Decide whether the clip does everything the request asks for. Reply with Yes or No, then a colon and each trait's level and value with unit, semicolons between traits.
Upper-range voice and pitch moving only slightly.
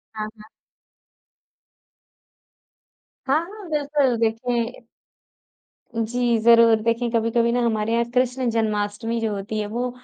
Yes: high, 230 Hz; narrow, 2.0 semitones